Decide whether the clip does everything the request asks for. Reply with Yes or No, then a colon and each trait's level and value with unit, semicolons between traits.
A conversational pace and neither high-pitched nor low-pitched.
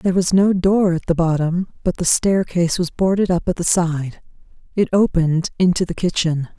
Yes: average, 190 wpm; medium, 175 Hz